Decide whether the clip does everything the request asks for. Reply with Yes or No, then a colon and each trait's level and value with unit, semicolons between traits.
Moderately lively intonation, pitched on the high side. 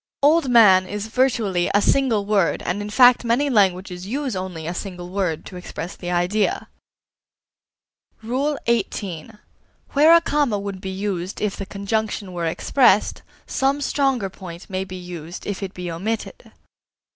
Yes: average, 4.6 semitones; high, 200 Hz